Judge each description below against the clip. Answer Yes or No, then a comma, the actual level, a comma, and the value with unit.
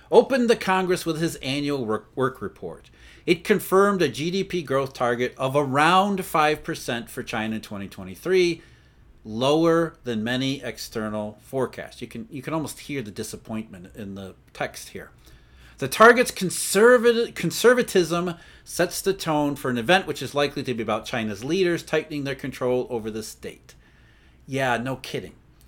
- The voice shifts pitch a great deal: Yes, wide, 6.6 semitones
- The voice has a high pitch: No, medium, 140 Hz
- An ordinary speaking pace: Yes, average, 150 wpm